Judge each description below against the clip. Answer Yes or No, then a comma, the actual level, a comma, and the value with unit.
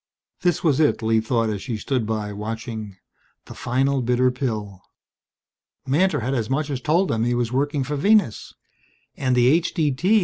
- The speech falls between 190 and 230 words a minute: No, average, 170 wpm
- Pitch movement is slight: No, average, 4.4 semitones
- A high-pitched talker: No, low, 125 Hz